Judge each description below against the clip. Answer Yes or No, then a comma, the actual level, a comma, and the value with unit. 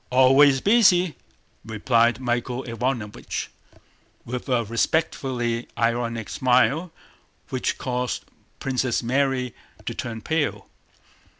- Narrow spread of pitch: Yes, narrow, 2.3 semitones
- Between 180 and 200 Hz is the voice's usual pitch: No, low, 125 Hz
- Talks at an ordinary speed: No, slow, 90 wpm